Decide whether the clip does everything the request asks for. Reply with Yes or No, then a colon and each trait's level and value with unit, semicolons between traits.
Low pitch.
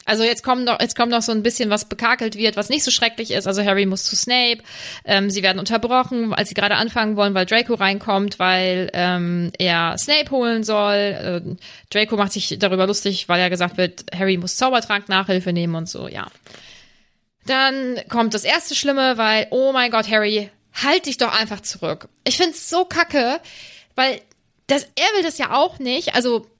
No: high, 220 Hz